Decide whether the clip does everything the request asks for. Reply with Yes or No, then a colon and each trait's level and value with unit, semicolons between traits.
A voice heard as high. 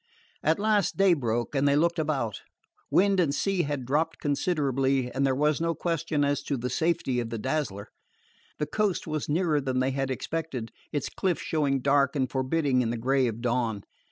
No: medium, 140 Hz